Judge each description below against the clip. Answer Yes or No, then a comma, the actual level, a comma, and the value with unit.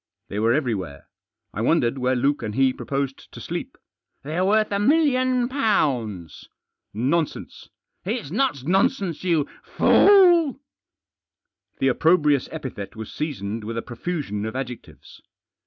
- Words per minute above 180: No, average, 140 wpm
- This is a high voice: No, medium, 145 Hz